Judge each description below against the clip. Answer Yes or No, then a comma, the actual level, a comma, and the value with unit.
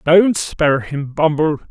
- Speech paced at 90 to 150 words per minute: Yes, average, 140 wpm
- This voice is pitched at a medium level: Yes, medium, 155 Hz